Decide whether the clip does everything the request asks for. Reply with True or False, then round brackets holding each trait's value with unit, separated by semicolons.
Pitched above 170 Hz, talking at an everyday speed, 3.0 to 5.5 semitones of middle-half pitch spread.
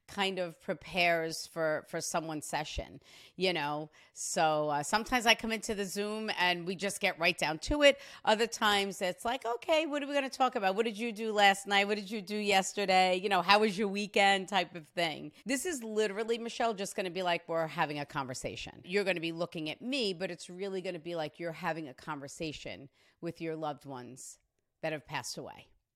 False (190 Hz; 215 wpm; 4.6 semitones)